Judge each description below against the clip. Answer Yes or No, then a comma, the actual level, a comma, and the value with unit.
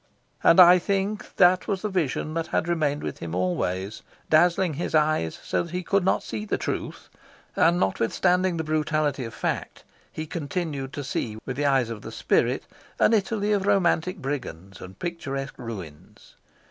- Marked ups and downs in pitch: Yes, wide, 6.2 semitones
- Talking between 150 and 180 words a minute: Yes, average, 170 wpm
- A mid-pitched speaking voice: Yes, medium, 155 Hz